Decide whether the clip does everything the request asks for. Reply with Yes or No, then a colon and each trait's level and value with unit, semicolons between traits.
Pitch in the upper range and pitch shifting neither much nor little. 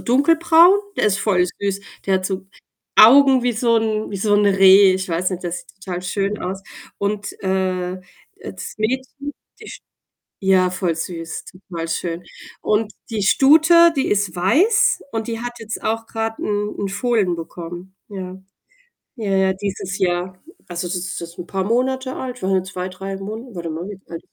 Yes: high, 195 Hz; average, 3.6 semitones